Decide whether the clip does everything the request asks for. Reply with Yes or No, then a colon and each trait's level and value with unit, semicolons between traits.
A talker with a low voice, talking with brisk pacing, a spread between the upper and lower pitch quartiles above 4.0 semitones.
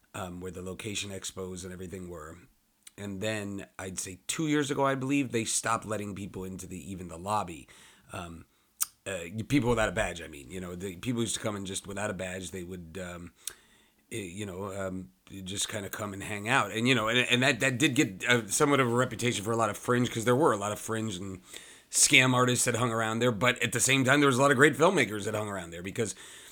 Yes: low, 105 Hz; fast, 245 wpm; average, 4.7 semitones